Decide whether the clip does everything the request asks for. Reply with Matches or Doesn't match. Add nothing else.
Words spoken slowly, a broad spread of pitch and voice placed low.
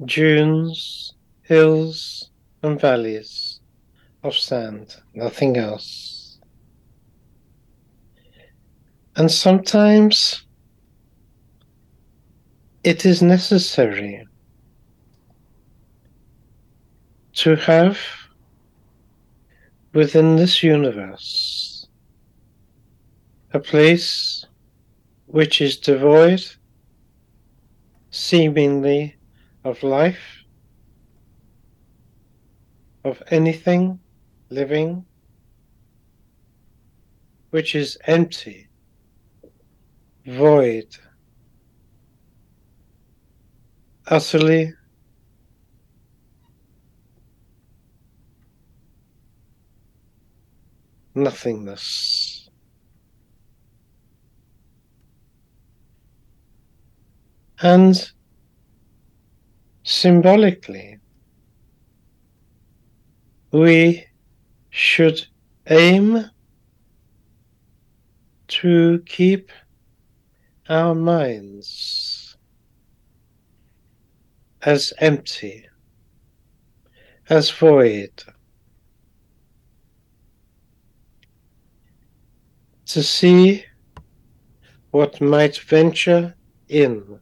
Matches